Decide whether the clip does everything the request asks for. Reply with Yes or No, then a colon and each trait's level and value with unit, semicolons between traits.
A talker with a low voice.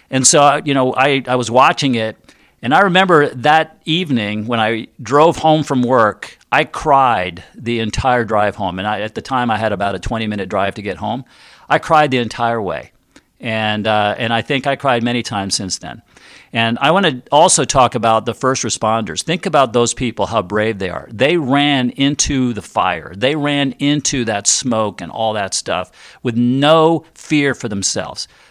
Yes: low, 120 Hz